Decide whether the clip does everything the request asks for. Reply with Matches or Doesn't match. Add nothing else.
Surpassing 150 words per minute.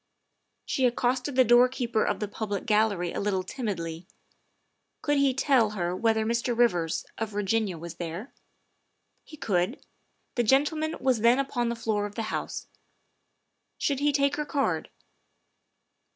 Doesn't match